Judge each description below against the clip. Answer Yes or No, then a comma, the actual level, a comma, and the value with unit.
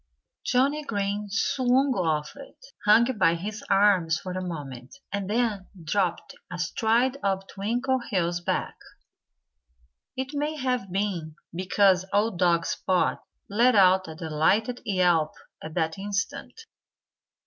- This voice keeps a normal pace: No, slow, 120 wpm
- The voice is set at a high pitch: Yes, high, 195 Hz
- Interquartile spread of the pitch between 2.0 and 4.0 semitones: No, average, 5.0 semitones